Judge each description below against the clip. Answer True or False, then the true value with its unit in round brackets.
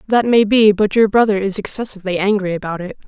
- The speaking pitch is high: True (205 Hz)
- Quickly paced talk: True (215 wpm)